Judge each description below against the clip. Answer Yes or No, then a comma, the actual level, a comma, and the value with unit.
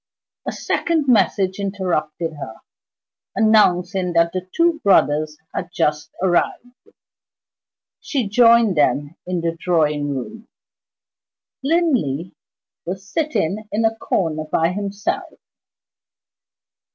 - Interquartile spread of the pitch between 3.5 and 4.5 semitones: No, wide, 5.4 semitones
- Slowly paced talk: Yes, slow, 100 wpm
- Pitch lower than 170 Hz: No, medium, 185 Hz